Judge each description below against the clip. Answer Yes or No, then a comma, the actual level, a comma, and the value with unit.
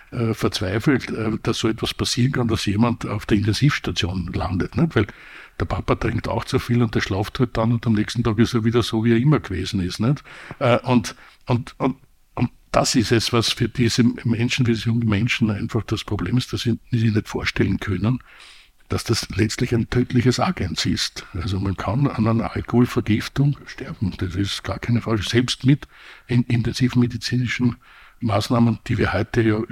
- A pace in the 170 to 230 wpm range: Yes, average, 185 wpm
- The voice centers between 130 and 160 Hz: No, low, 115 Hz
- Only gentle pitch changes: Yes, narrow, 2.3 semitones